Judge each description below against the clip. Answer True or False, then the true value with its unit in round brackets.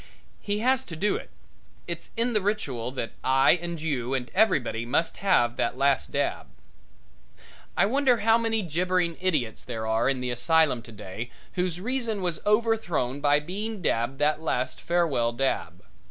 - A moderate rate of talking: True (160 wpm)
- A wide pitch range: True (8.5 semitones)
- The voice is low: False (160 Hz)